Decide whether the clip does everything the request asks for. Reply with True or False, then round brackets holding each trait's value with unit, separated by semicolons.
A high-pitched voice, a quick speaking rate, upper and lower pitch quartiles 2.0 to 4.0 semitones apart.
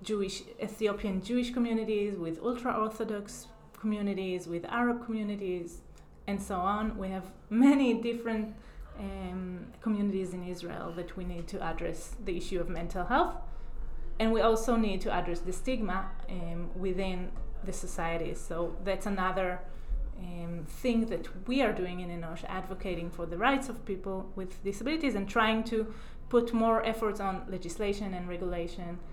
False (195 Hz; 150 wpm; 3.6 semitones)